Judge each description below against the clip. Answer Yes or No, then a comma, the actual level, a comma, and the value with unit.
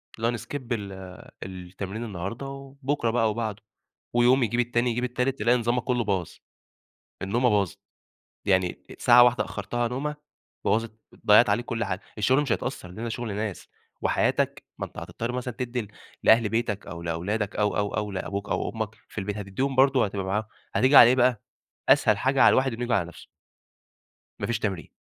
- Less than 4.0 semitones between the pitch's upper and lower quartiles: Yes, average, 3.4 semitones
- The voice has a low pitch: Yes, low, 115 Hz